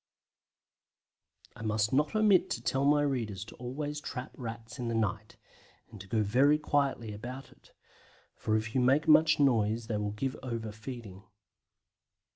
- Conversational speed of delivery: Yes, average, 160 wpm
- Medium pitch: No, low, 120 Hz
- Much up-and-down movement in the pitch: No, average, 4.4 semitones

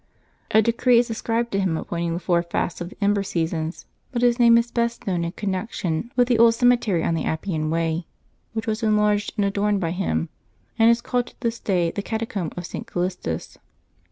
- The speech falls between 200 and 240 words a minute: Yes, fast, 205 wpm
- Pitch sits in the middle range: No, high, 200 Hz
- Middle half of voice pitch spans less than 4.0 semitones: No, average, 5.2 semitones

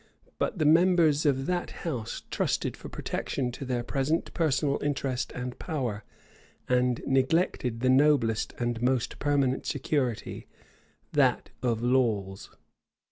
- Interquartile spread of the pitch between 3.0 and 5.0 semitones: Yes, average, 3.3 semitones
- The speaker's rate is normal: No, slow, 125 wpm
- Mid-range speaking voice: No, low, 130 Hz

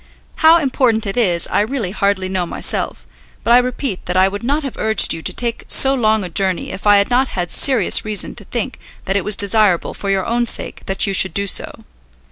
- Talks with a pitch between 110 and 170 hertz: No, high, 205 Hz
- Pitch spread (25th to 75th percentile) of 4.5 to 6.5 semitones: No, average, 4.1 semitones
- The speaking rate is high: Yes, fast, 230 wpm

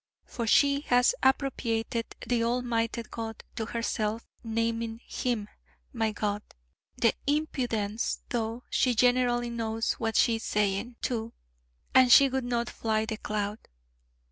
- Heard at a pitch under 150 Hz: No, high, 230 Hz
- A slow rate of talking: Yes, slow, 130 wpm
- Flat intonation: Yes, narrow, 1.8 semitones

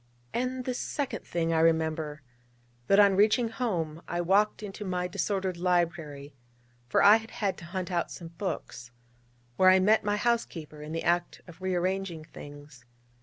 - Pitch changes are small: No, average, 4.0 semitones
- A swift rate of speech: No, average, 165 wpm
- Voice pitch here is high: No, medium, 180 Hz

